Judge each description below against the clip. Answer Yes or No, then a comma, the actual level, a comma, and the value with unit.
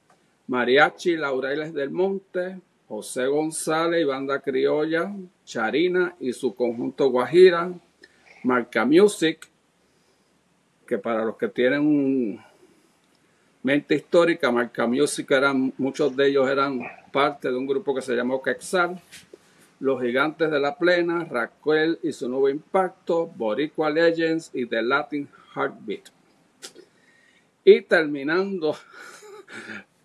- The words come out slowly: Yes, slow, 110 wpm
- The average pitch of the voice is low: No, medium, 150 Hz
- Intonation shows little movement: No, average, 4.6 semitones